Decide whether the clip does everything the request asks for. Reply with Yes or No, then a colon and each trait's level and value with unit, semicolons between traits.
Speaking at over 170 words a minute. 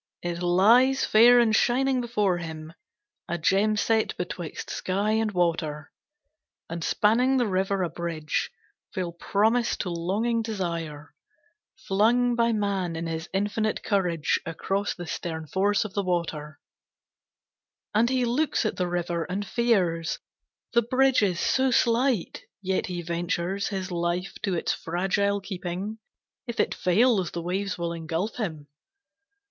No: average, 140 wpm